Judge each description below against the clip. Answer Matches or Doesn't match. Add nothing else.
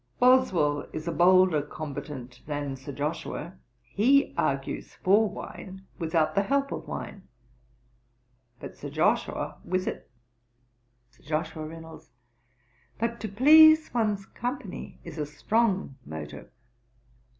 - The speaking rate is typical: Doesn't match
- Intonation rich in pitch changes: Matches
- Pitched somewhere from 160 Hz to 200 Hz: Matches